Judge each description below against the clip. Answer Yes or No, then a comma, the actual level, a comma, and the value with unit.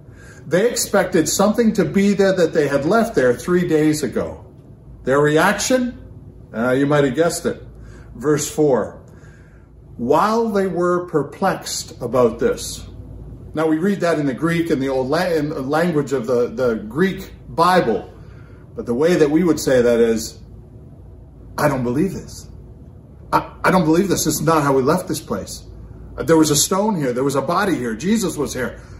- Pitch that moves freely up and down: Yes, wide, 5.9 semitones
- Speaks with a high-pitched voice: No, medium, 150 Hz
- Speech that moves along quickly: No, average, 175 wpm